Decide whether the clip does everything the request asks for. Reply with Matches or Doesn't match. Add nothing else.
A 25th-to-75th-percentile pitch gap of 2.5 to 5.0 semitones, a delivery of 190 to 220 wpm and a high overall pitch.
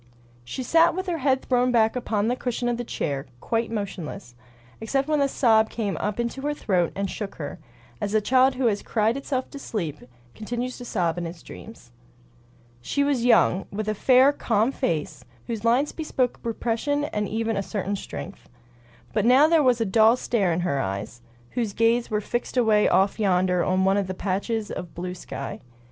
Matches